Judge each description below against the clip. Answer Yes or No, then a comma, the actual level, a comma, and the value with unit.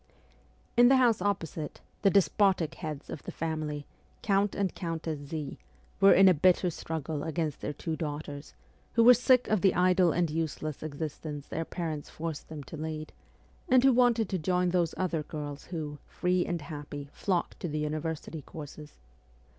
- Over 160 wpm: Yes, average, 170 wpm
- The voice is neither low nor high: Yes, medium, 160 Hz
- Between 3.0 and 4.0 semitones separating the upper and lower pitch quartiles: Yes, average, 3.5 semitones